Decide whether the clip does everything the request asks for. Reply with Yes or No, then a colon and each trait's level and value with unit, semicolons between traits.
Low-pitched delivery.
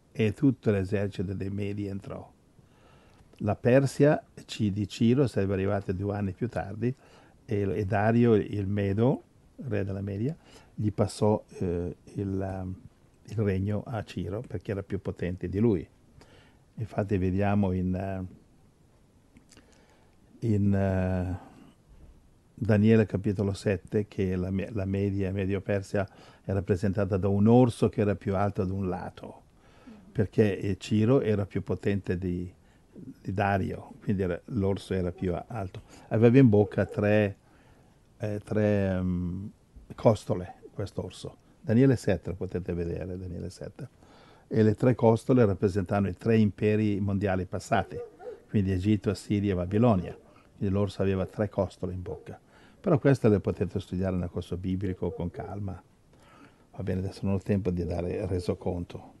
Yes: low, 100 Hz